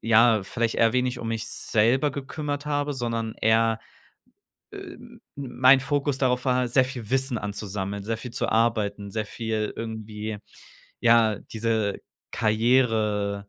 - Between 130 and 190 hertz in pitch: No, low, 115 Hz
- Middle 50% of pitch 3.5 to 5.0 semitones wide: No, average, 3.0 semitones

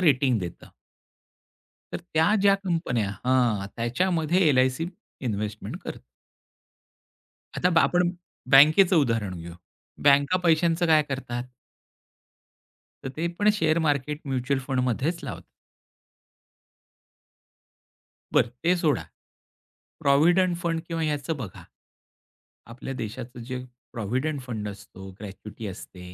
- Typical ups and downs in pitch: No, wide, 5.7 semitones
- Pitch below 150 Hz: Yes, medium, 140 Hz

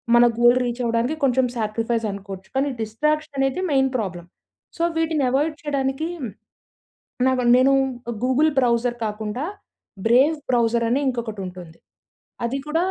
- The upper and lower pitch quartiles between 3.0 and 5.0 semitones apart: Yes, average, 3.4 semitones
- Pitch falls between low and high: No, high, 245 Hz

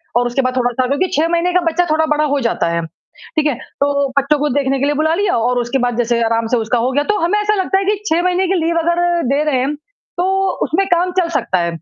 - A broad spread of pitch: Yes, wide, 6.0 semitones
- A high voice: Yes, very high, 295 Hz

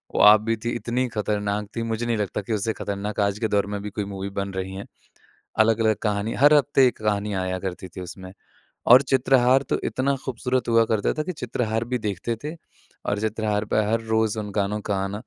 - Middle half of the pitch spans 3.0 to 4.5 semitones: No, narrow, 2.6 semitones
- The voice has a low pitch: Yes, low, 110 Hz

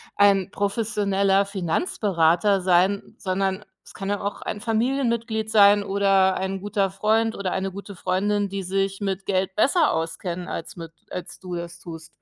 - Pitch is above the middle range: Yes, high, 195 Hz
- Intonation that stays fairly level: Yes, narrow, 1.7 semitones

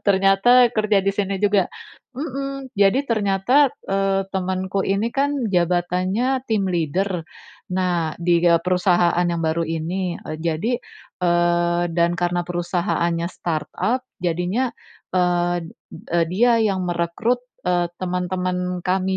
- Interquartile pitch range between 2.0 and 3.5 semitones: Yes, narrow, 2.6 semitones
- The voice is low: No, medium, 185 Hz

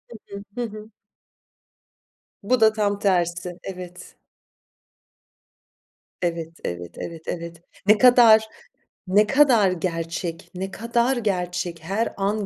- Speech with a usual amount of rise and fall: Yes, average, 4.0 semitones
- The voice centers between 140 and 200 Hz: Yes, high, 195 Hz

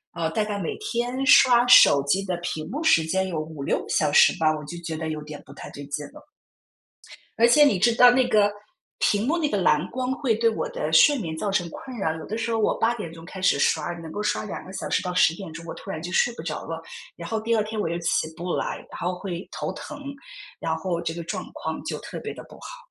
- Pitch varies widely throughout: Yes, wide, 6.0 semitones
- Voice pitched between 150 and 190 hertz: Yes, medium, 185 Hz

